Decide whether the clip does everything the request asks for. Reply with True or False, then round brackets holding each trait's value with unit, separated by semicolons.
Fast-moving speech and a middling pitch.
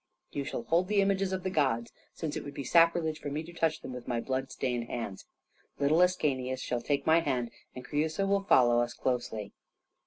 True (210 wpm; 145 Hz)